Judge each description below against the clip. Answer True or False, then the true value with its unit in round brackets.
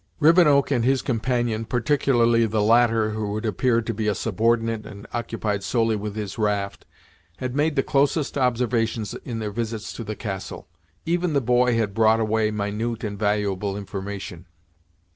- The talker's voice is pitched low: True (115 Hz)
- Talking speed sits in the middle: True (160 wpm)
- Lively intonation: False (2.6 semitones)